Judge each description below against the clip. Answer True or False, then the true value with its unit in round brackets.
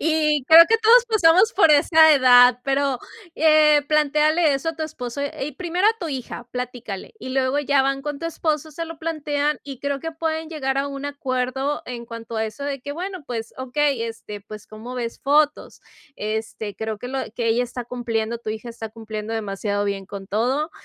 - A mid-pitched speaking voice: False (275 Hz)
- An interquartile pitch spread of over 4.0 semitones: True (4.8 semitones)